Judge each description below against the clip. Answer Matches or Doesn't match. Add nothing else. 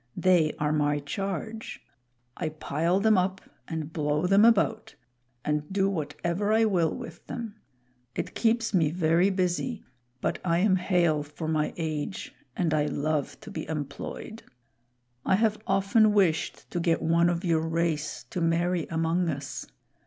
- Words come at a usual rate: Matches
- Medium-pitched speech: Matches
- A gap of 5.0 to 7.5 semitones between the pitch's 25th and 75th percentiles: Doesn't match